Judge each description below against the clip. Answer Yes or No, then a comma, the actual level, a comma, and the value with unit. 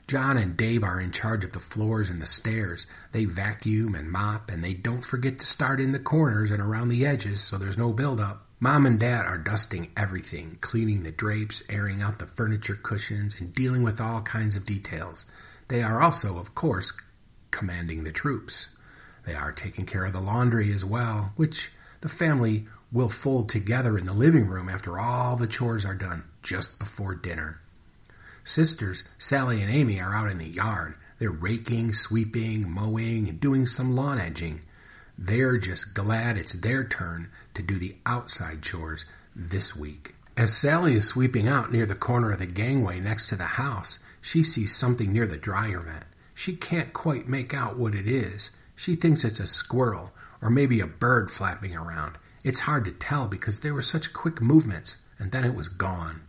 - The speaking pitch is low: Yes, low, 110 Hz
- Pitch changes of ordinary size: Yes, average, 4.4 semitones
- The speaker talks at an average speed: Yes, average, 190 wpm